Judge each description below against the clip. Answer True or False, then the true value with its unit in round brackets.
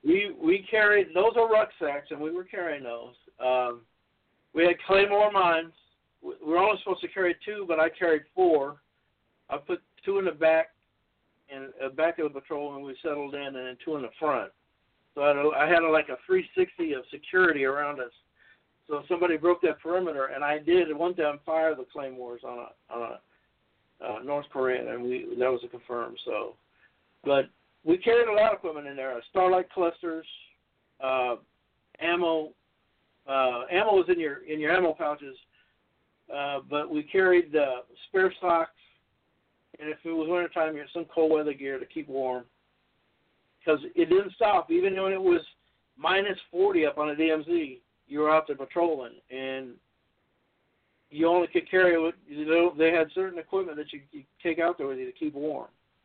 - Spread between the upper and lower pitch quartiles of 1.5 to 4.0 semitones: False (4.8 semitones)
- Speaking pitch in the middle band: True (160 Hz)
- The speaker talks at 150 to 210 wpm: True (190 wpm)